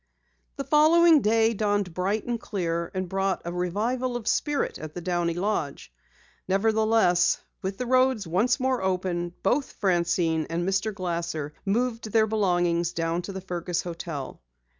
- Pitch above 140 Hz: Yes, high, 190 Hz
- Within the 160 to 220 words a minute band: No, average, 150 wpm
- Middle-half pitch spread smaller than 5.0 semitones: Yes, average, 4.5 semitones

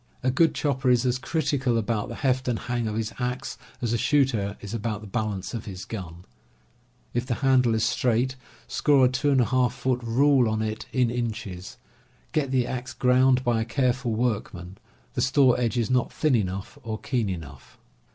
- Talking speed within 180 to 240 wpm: Yes, average, 190 wpm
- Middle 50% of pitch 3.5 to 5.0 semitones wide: No, average, 2.9 semitones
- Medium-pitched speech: No, low, 120 Hz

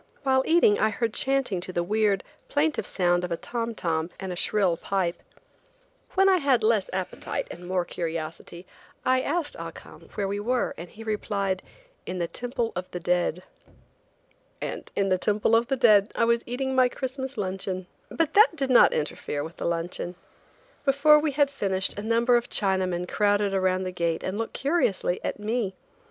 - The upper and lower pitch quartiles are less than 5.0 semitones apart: No, wide, 5.5 semitones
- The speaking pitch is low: No, high, 205 Hz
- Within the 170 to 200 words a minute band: Yes, average, 185 wpm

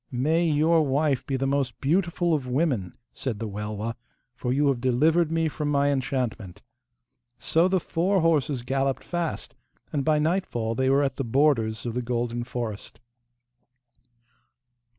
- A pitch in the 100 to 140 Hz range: Yes, low, 135 Hz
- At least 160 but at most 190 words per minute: No, average, 150 wpm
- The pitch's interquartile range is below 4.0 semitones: No, average, 4.6 semitones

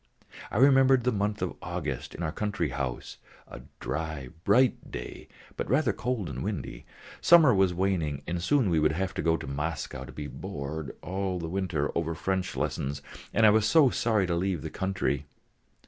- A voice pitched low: Yes, very low, 90 Hz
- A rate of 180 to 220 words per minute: Yes, average, 185 wpm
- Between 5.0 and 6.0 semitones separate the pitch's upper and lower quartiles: Yes, wide, 5.6 semitones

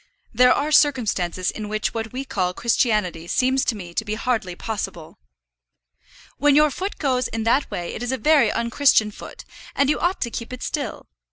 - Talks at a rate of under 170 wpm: No, average, 190 wpm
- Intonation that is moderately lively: Yes, average, 4.4 semitones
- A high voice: Yes, high, 235 Hz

